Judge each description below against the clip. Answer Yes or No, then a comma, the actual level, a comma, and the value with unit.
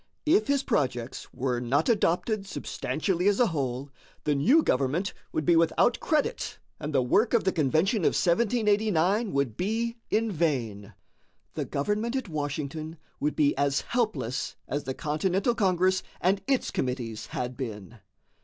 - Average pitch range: No, wide, 7.6 semitones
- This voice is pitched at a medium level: Yes, medium, 165 Hz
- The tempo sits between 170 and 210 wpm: No, average, 150 wpm